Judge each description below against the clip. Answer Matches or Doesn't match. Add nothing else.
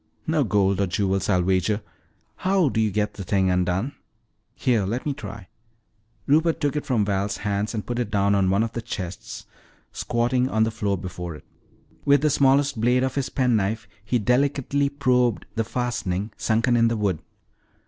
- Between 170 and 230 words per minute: Matches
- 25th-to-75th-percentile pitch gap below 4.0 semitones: Doesn't match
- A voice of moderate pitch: Doesn't match